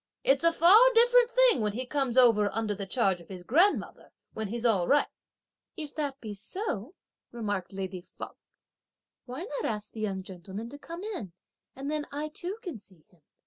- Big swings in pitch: Yes, wide, 8.2 semitones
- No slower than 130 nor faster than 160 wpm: No, average, 185 wpm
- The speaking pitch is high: Yes, high, 240 Hz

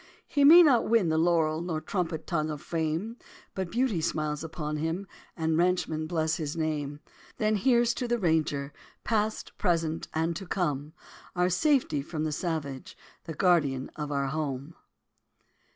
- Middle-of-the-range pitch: Yes, medium, 160 Hz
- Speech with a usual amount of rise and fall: Yes, average, 3.3 semitones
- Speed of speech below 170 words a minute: Yes, average, 160 wpm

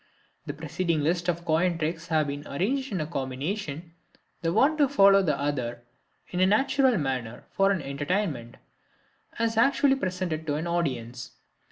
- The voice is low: No, medium, 165 Hz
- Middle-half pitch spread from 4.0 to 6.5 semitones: Yes, average, 5.3 semitones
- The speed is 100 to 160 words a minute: Yes, average, 155 wpm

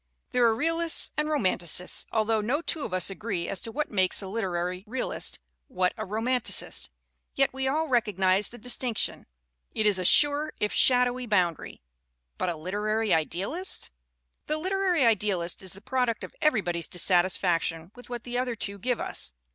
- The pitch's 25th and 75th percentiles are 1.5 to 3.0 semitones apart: No, wide, 5.5 semitones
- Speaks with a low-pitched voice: No, high, 220 Hz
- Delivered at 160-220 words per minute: Yes, average, 175 wpm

